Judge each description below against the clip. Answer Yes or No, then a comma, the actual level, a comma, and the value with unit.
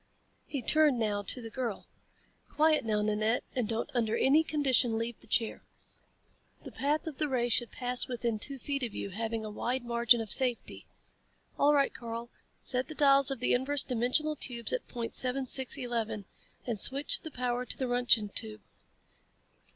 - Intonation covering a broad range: No, average, 3.1 semitones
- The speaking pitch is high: Yes, high, 245 Hz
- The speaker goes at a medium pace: Yes, average, 180 wpm